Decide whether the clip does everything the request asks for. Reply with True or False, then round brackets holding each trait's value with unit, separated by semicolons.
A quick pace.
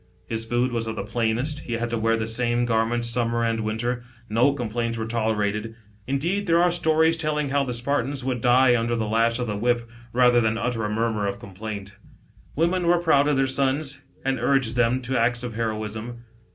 True (210 wpm)